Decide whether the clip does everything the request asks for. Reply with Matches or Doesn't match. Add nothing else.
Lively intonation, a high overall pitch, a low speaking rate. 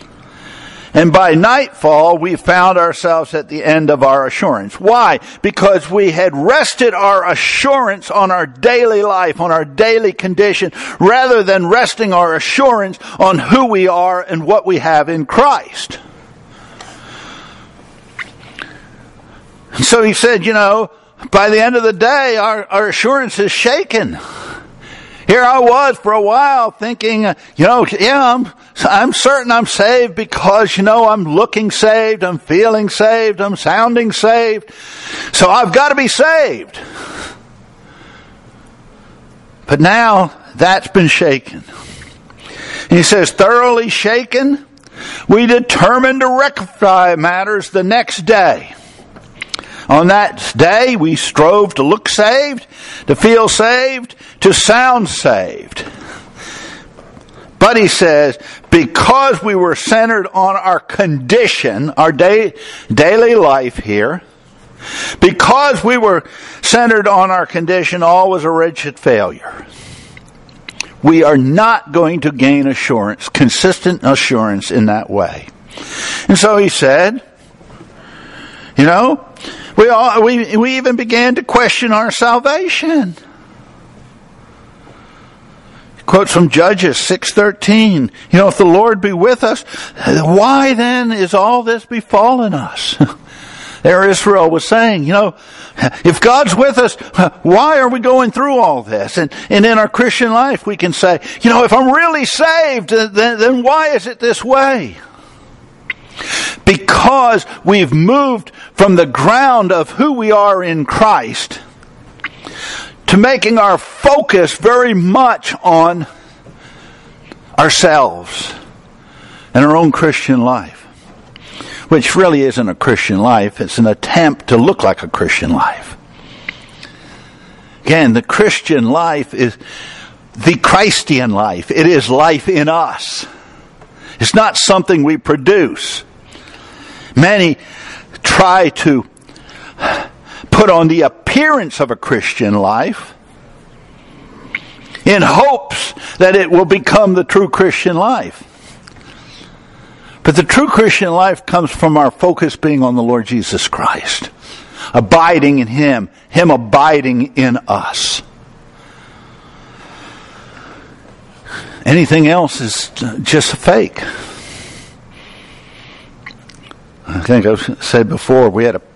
Matches